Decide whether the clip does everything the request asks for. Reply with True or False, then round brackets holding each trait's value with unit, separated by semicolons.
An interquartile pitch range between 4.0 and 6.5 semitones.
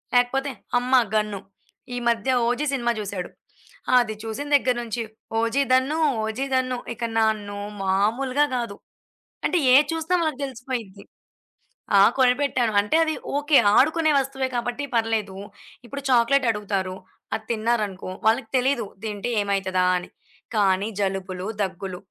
True (4.5 semitones)